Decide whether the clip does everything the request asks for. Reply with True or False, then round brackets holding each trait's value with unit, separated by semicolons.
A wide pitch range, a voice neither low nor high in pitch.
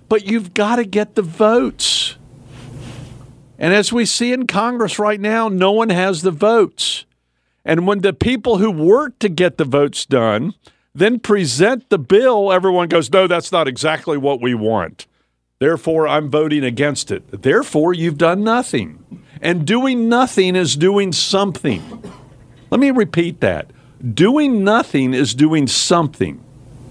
True (7.0 semitones; 175 Hz)